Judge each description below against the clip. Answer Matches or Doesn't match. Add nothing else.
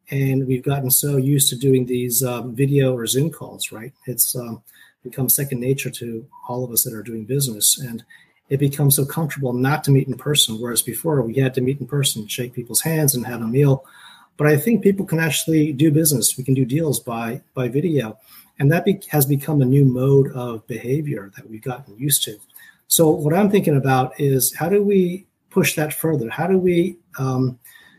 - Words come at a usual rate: Doesn't match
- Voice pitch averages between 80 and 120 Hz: Doesn't match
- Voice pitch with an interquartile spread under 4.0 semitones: Matches